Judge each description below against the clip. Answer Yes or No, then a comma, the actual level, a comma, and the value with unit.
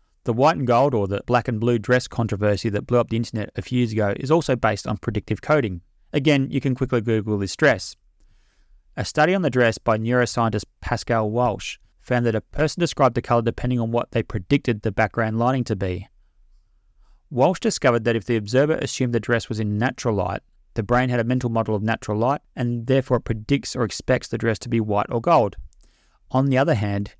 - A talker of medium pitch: No, low, 120 Hz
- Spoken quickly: Yes, fast, 215 wpm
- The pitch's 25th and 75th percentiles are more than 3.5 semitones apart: No, average, 3.1 semitones